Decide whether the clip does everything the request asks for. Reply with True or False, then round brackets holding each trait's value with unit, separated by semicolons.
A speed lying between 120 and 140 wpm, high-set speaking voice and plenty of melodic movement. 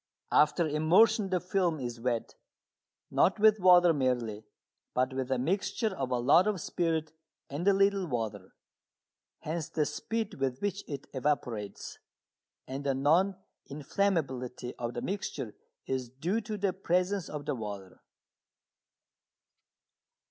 False (135 wpm; 150 Hz; 6.7 semitones)